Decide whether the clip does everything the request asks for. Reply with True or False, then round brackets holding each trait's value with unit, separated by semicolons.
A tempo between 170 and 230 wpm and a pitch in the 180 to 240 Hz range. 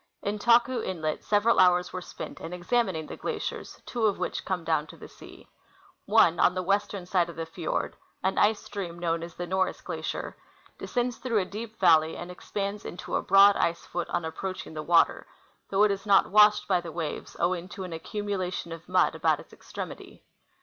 True (200 wpm; 185 Hz)